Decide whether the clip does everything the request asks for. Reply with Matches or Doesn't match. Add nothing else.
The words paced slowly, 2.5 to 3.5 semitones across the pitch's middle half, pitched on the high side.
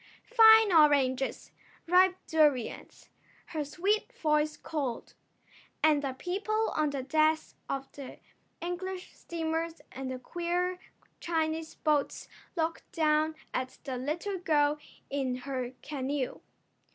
Doesn't match